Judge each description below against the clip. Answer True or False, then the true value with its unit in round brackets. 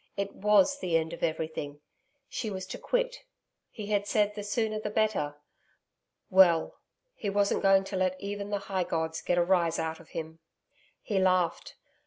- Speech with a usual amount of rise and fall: True (3.5 semitones)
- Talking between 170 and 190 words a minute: True (175 wpm)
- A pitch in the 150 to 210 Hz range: True (190 Hz)